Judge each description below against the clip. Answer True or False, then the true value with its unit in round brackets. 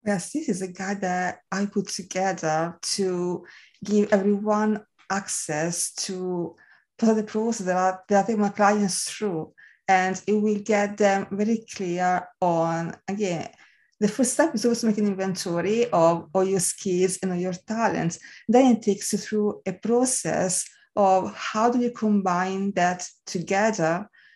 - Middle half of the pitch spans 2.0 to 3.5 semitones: True (2.7 semitones)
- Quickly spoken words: False (160 wpm)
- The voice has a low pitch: False (195 Hz)